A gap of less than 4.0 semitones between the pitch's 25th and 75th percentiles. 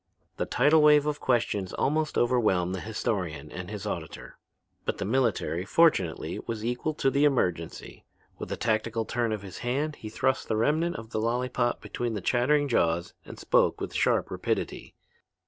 No: average, 5.2 semitones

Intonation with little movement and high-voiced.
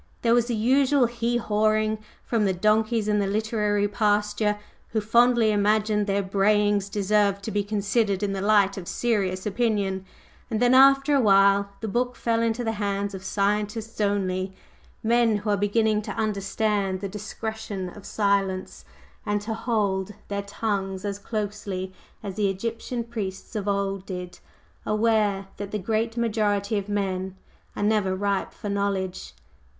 Yes: narrow, 1.9 semitones; high, 210 Hz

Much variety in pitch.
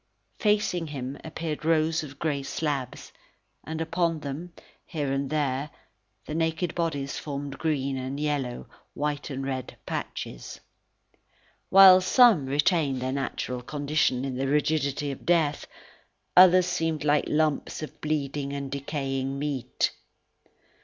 No: average, 2.8 semitones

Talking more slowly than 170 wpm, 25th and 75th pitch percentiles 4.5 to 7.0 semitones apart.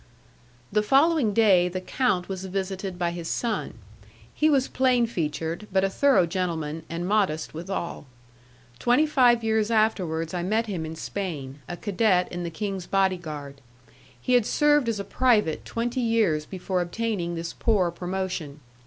Yes: average, 160 wpm; average, 4.9 semitones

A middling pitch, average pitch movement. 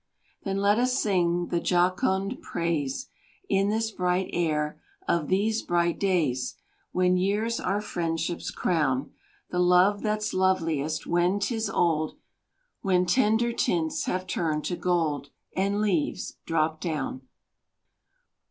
Yes: medium, 180 Hz; average, 3.5 semitones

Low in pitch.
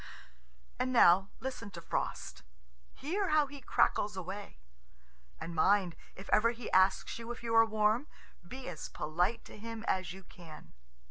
No: high, 210 Hz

